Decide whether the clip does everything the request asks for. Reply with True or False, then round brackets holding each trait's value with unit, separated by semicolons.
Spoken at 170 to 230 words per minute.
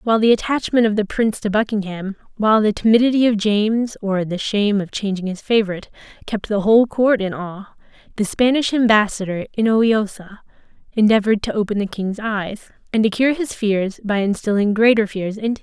True (180 wpm)